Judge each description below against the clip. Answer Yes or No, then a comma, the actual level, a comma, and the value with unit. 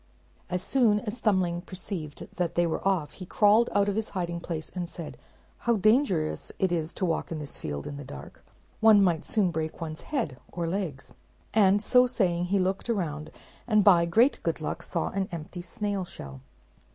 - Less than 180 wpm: No, average, 190 wpm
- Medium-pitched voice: Yes, medium, 180 Hz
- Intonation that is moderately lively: Yes, average, 3.9 semitones